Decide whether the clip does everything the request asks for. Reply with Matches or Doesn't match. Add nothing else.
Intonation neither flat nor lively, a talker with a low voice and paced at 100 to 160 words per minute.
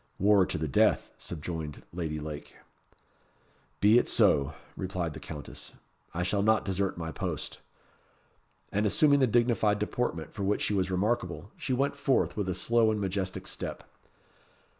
Matches